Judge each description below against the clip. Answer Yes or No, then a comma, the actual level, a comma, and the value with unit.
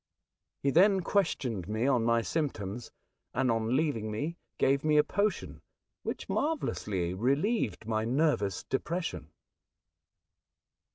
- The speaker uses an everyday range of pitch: No, wide, 6.7 semitones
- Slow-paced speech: Yes, slow, 115 wpm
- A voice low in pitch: Yes, low, 130 Hz